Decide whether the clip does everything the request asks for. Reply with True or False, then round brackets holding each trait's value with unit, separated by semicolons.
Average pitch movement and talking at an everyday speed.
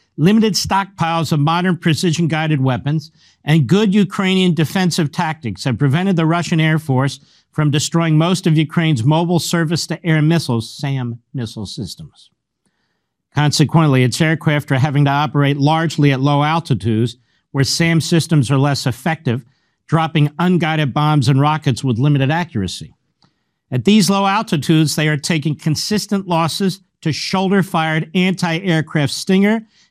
False (3.2 semitones; 130 wpm)